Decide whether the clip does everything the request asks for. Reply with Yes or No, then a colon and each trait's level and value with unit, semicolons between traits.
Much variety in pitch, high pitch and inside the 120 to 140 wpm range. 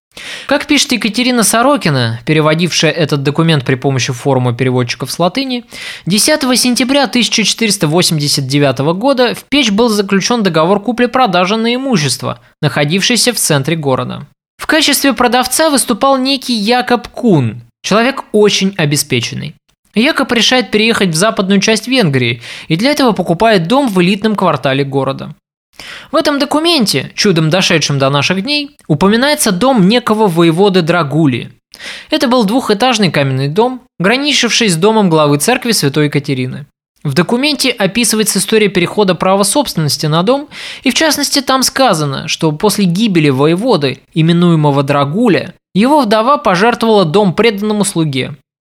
Yes: wide, 7.8 semitones; high, 205 Hz; average, 130 wpm